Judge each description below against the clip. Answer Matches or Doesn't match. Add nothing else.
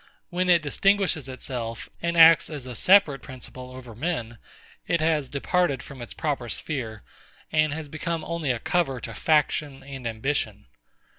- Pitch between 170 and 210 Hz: Doesn't match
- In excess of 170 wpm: Doesn't match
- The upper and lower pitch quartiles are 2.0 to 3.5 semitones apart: Doesn't match